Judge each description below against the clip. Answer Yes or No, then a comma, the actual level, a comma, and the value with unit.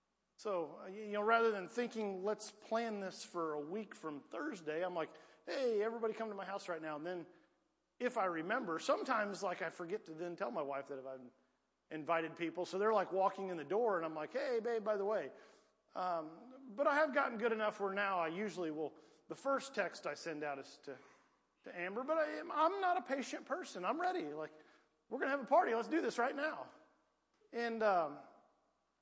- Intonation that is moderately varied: No, wide, 6.2 semitones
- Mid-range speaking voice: No, high, 205 Hz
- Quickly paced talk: Yes, fast, 210 wpm